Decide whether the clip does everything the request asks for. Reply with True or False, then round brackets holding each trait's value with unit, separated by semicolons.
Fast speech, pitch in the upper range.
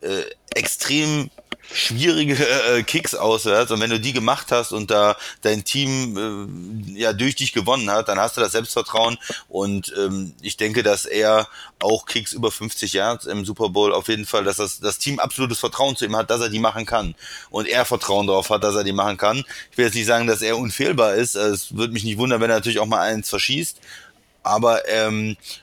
False (215 wpm; 110 Hz)